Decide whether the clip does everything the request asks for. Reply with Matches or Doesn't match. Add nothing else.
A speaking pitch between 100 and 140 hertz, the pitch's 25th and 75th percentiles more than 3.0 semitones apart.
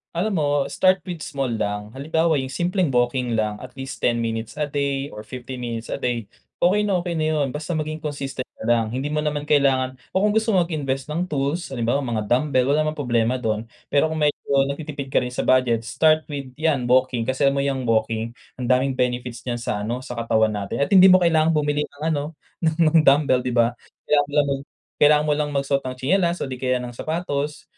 Matches